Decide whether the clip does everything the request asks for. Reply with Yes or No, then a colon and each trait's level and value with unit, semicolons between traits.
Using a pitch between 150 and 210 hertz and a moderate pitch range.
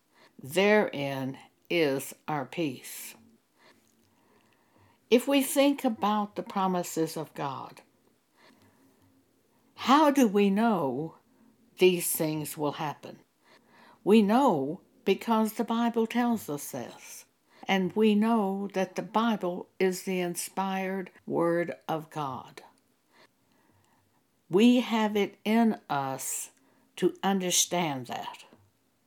No: high, 190 Hz; wide, 5.7 semitones